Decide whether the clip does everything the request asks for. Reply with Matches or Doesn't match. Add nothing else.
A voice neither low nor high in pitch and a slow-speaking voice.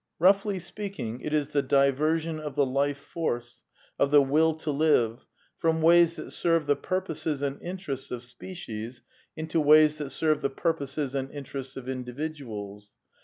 Doesn't match